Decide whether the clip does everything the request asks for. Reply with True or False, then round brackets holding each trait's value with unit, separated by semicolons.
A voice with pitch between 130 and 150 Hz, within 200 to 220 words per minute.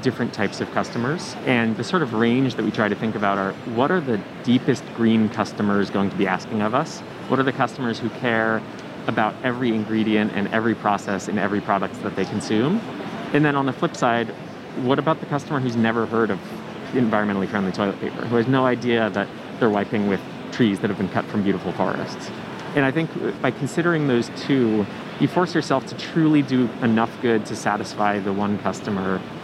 False (115 Hz; 205 wpm)